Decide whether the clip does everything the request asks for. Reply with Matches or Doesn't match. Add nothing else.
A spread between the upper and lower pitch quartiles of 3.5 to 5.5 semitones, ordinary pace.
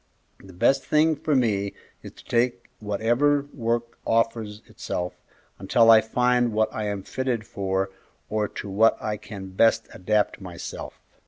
Doesn't match